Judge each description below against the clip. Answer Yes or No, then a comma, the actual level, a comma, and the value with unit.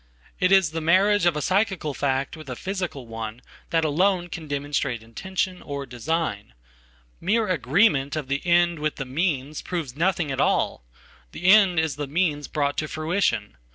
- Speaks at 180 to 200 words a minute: No, average, 155 wpm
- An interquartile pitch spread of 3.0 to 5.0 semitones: Yes, average, 4.7 semitones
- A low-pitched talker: No, medium, 155 Hz